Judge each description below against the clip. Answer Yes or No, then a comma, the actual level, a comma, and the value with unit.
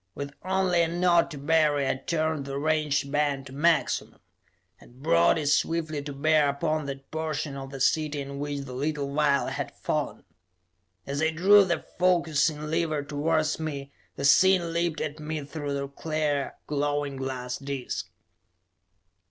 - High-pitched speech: No, medium, 150 Hz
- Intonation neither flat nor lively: No, narrow, 2.3 semitones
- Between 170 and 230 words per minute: No, average, 160 wpm